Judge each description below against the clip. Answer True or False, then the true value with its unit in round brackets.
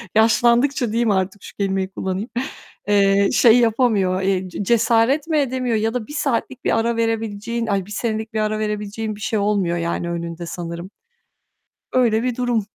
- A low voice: False (215 Hz)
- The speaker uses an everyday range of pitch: True (3.2 semitones)